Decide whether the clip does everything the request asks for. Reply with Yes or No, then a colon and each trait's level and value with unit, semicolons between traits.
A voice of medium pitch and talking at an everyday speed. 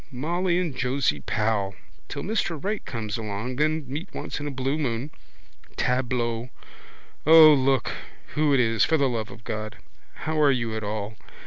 No: low, 130 Hz; average, 165 wpm